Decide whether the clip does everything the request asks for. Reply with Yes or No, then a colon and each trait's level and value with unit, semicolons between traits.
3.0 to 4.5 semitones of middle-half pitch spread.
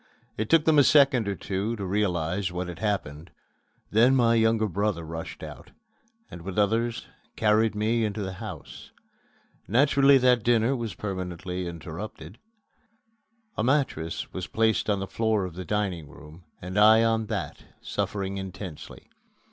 Yes: average, 3.7 semitones